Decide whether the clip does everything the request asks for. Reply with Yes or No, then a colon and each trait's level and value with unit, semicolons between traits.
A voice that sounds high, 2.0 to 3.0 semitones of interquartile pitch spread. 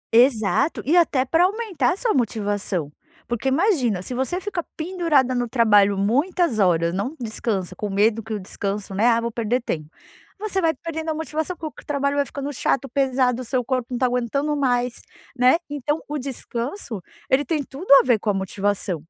No: very high, 255 Hz; wide, 5.4 semitones